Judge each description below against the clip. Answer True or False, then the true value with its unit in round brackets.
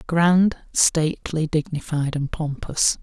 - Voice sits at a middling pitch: True (160 Hz)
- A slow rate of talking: True (100 wpm)